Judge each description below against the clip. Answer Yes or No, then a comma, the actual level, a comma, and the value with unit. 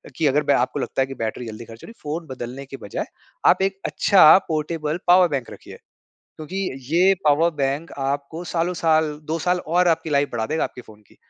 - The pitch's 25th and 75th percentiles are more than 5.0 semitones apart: No, average, 3.7 semitones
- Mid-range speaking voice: Yes, medium, 155 Hz